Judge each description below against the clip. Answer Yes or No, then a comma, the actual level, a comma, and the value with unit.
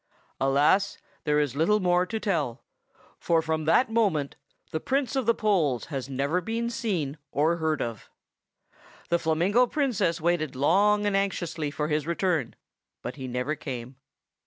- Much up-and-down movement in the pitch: Yes, wide, 5.7 semitones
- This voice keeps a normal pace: Yes, average, 155 wpm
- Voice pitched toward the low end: No, medium, 165 Hz